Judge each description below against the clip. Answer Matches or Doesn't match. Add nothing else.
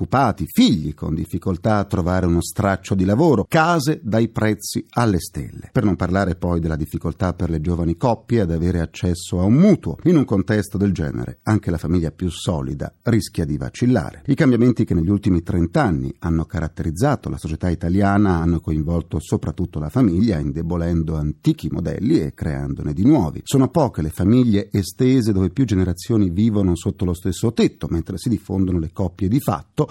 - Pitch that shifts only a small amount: Doesn't match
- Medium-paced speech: Doesn't match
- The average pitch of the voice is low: Matches